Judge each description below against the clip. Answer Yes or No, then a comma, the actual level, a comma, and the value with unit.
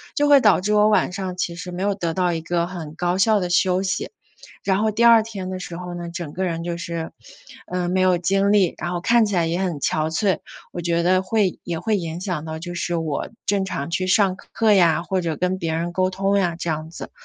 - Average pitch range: No, narrow, 2.3 semitones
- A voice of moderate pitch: Yes, medium, 180 Hz